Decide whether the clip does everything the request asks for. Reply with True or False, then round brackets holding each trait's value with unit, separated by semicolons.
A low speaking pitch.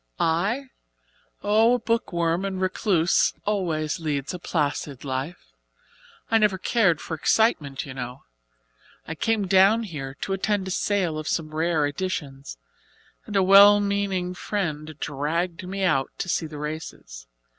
False (175 Hz)